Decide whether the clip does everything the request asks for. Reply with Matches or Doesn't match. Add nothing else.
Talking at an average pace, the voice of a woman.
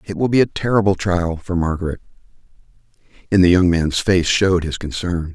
Doesn't match